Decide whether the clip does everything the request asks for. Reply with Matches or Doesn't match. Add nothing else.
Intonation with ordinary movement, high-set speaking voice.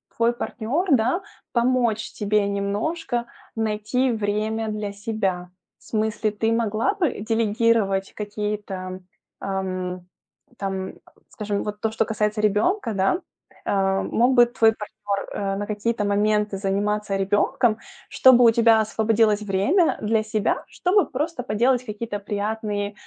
Doesn't match